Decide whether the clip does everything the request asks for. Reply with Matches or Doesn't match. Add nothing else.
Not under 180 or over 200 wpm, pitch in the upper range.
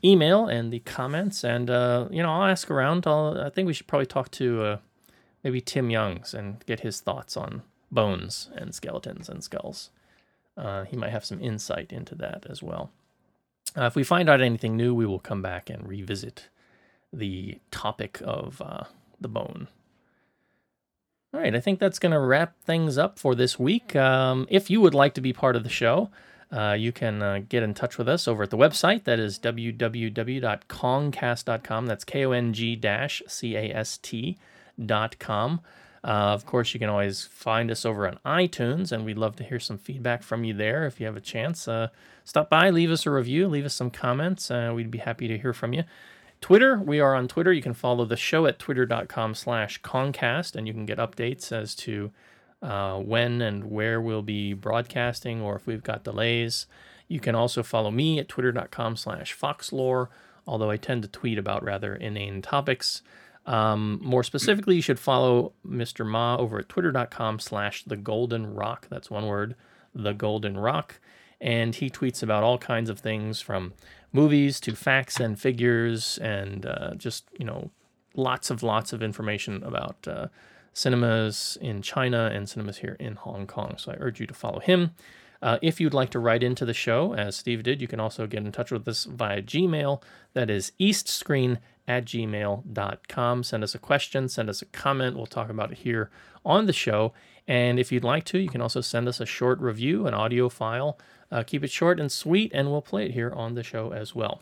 Doesn't match